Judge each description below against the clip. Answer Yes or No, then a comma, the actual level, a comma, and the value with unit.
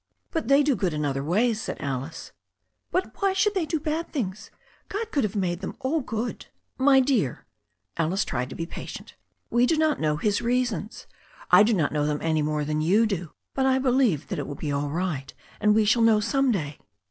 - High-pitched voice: Yes, high, 210 Hz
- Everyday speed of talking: No, fast, 225 wpm